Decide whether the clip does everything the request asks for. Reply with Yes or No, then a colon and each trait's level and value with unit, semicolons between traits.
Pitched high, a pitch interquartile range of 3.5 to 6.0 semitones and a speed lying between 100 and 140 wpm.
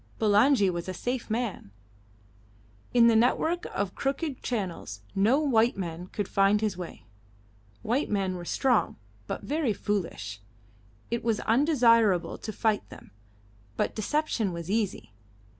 Yes: high, 215 Hz; average, 4.6 semitones; slow, 135 wpm